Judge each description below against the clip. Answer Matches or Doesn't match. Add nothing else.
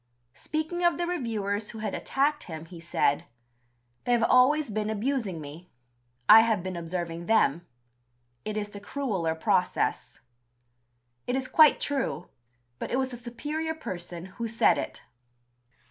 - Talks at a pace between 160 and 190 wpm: Doesn't match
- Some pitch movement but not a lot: Doesn't match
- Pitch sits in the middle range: Doesn't match